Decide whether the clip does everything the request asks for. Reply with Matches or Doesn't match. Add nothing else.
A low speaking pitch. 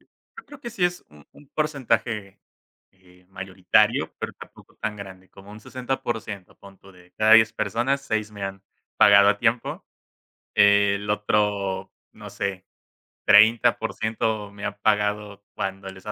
Matches